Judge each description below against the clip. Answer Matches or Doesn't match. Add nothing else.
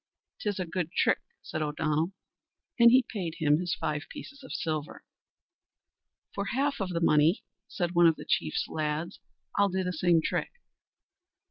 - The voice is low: Doesn't match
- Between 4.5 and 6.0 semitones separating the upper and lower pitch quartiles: Doesn't match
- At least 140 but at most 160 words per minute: Matches